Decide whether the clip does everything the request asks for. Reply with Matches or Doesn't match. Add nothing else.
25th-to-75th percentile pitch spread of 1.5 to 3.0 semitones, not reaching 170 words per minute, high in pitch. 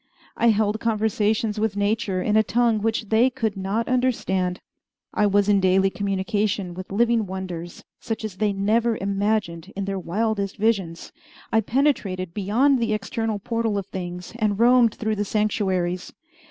Matches